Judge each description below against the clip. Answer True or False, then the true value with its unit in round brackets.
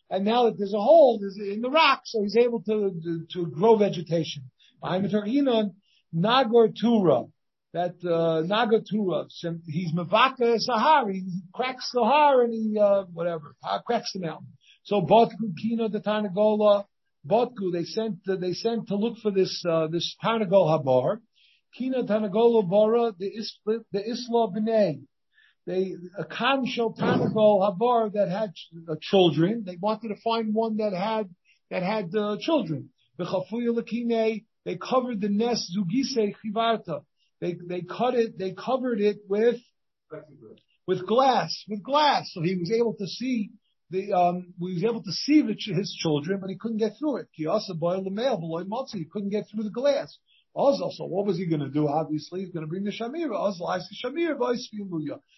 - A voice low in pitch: False (210 Hz)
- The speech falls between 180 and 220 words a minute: False (155 wpm)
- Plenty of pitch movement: False (4.2 semitones)